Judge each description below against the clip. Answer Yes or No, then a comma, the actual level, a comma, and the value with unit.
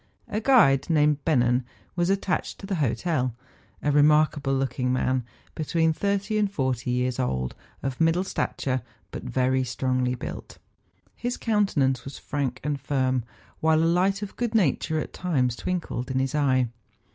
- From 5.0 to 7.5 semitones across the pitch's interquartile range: Yes, average, 5.3 semitones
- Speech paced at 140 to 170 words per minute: Yes, average, 155 wpm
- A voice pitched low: No, medium, 145 Hz